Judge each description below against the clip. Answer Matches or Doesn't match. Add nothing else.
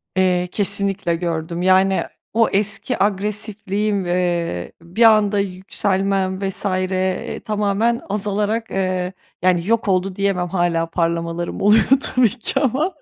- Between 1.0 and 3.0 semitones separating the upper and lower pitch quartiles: Matches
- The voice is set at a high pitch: Matches